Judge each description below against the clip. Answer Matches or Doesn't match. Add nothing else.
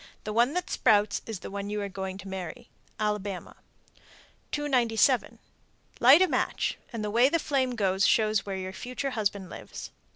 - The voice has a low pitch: Doesn't match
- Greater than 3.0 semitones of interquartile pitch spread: Matches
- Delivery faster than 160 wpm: Matches